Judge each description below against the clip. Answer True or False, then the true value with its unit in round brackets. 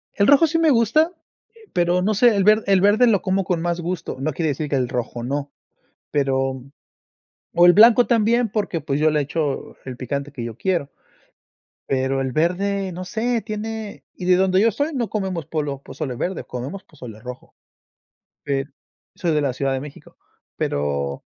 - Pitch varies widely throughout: True (7.4 semitones)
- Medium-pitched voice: True (175 Hz)